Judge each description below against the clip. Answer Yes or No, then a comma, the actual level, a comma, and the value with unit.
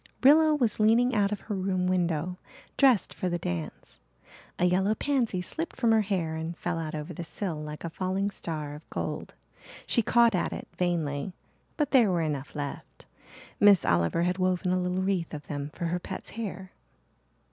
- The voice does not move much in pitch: No, average, 4.3 semitones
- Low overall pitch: No, medium, 180 Hz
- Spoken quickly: No, average, 185 wpm